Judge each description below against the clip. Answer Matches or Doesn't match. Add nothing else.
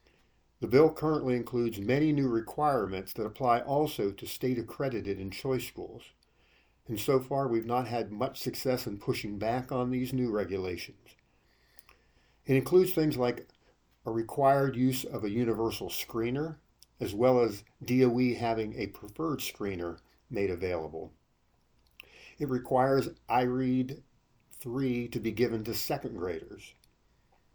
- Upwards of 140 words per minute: Doesn't match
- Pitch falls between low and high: Doesn't match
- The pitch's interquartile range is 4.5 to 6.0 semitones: Doesn't match